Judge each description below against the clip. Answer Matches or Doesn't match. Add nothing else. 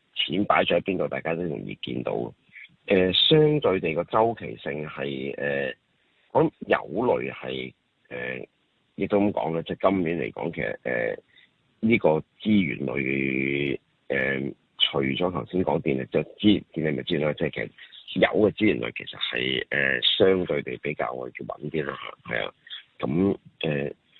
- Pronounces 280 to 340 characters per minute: Doesn't match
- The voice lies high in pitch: Doesn't match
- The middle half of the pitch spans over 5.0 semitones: Matches